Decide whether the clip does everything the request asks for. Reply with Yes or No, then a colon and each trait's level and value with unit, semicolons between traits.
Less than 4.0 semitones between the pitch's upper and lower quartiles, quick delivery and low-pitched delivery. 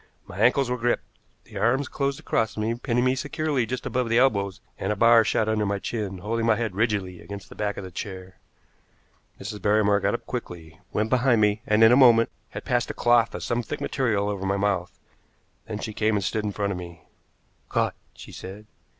Yes: average, 3.0 semitones; fast, 215 wpm; low, 110 Hz